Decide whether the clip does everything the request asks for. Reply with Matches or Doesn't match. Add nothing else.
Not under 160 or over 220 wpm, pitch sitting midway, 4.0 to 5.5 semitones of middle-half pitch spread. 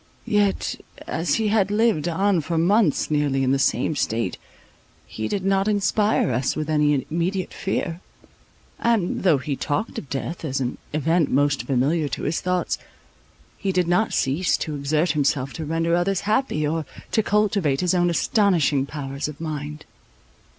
Matches